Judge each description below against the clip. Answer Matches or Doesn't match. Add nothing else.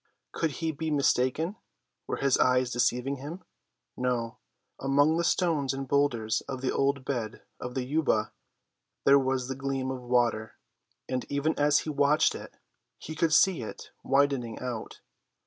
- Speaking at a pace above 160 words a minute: Doesn't match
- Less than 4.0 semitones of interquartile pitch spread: Matches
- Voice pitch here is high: Doesn't match